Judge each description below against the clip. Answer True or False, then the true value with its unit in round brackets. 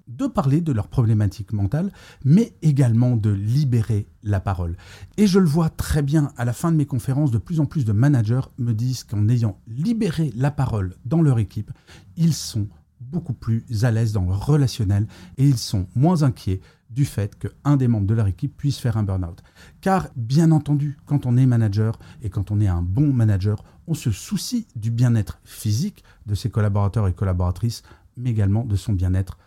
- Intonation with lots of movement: True (5.8 semitones)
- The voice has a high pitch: False (120 Hz)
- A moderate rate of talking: True (195 wpm)